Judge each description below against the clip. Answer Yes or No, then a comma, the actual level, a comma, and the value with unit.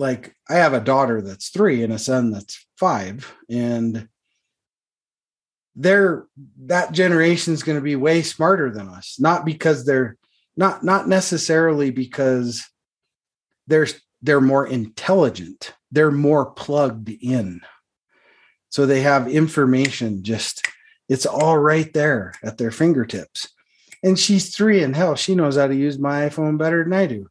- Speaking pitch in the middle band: Yes, medium, 145 Hz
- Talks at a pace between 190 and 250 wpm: No, average, 145 wpm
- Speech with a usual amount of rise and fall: Yes, average, 4.6 semitones